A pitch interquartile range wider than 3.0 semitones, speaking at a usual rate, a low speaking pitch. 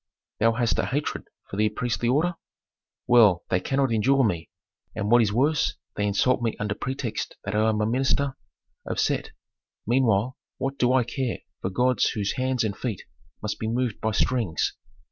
Yes: average, 3.5 semitones; average, 180 wpm; low, 115 Hz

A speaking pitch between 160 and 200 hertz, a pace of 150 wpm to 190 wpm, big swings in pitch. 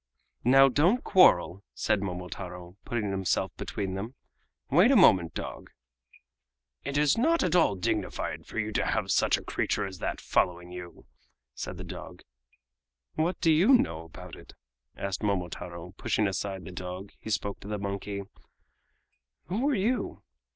No: low, 100 Hz; average, 160 wpm; wide, 9.0 semitones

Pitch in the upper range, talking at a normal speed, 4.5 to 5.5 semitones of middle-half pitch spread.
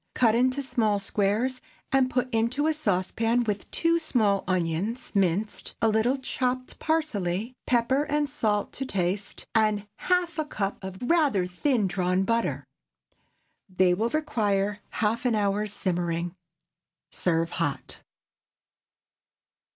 No: high, 220 Hz; slow, 125 wpm; average, 4.9 semitones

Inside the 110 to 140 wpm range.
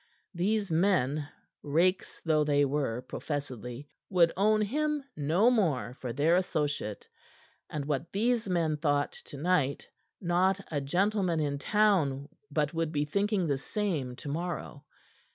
Yes: slow, 135 wpm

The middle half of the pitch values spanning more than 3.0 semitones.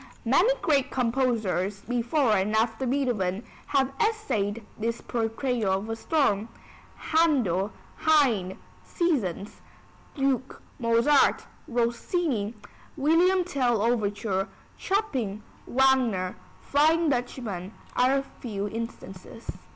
Yes: average, 4.8 semitones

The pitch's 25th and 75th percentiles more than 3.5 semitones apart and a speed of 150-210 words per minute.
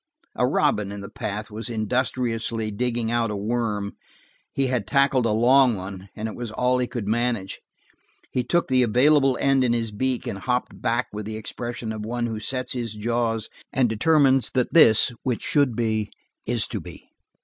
No: average, 2.7 semitones; average, 185 wpm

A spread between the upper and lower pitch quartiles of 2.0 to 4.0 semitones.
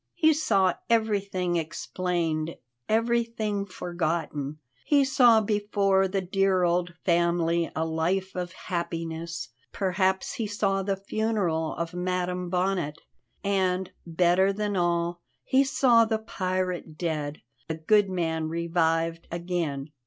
Yes: average, 3.0 semitones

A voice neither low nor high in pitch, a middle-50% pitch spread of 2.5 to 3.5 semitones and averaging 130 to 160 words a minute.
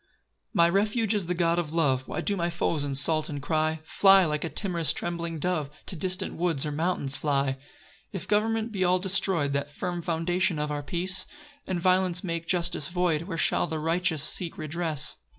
No: medium, 170 Hz; average, 3.1 semitones; average, 195 wpm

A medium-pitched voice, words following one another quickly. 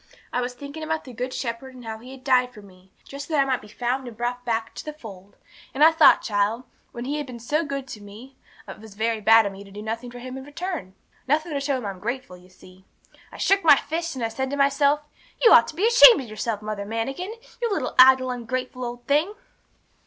No: very high, 250 Hz; fast, 250 wpm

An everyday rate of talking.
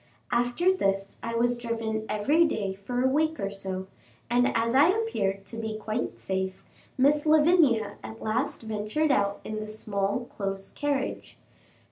Yes: average, 155 wpm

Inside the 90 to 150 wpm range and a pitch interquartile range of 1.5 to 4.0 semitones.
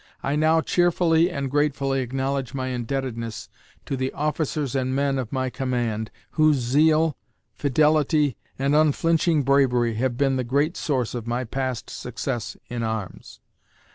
Yes: average, 140 wpm; average, 3.2 semitones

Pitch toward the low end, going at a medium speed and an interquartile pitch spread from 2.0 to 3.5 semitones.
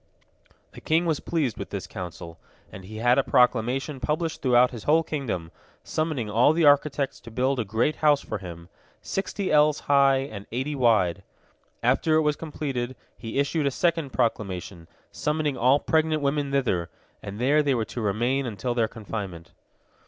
No: low, 130 Hz; average, 175 wpm; average, 5.2 semitones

